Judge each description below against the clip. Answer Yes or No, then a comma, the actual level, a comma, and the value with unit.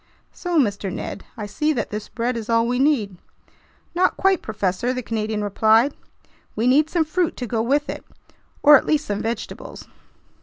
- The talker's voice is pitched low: No, high, 235 Hz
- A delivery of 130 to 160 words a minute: No, average, 180 wpm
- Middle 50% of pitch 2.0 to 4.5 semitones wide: No, wide, 5.6 semitones